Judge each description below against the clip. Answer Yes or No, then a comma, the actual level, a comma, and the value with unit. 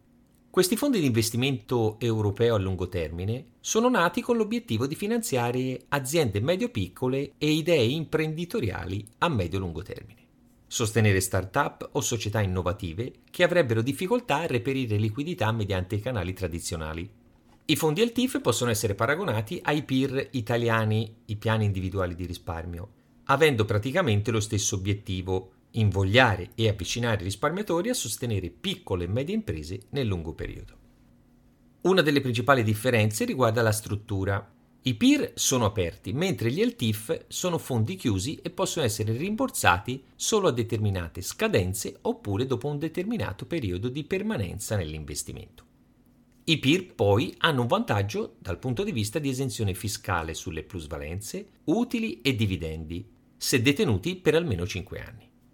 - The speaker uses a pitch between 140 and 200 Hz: No, low, 115 Hz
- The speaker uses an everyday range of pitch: No, wide, 6.0 semitones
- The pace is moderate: Yes, average, 135 wpm